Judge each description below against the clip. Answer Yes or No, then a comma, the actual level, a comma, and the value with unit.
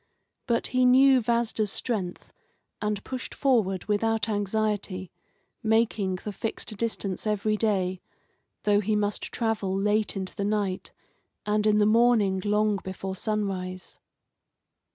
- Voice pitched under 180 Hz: No, high, 210 Hz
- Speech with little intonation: Yes, narrow, 2.3 semitones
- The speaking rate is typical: No, slow, 125 wpm